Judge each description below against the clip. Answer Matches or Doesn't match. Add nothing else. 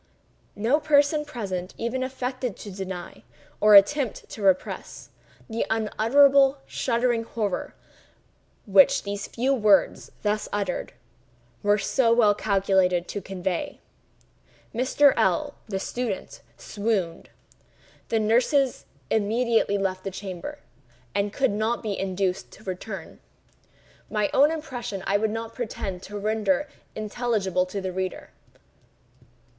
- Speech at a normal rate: Doesn't match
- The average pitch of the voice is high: Matches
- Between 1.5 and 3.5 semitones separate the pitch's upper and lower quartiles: Doesn't match